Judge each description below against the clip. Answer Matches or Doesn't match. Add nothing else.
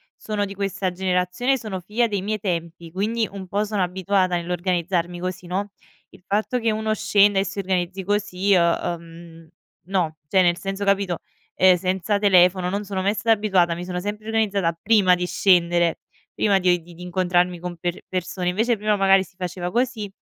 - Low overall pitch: Doesn't match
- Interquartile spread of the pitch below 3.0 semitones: Matches